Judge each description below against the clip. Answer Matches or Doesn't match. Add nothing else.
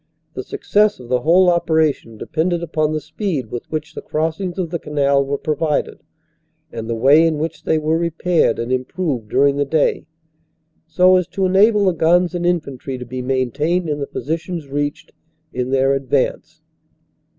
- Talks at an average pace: Matches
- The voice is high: Doesn't match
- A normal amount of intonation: Matches